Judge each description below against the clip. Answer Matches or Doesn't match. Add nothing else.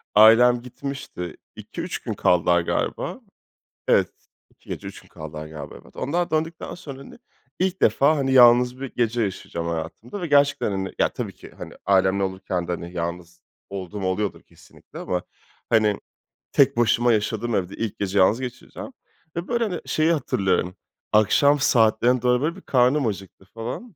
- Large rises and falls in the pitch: Matches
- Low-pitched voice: Matches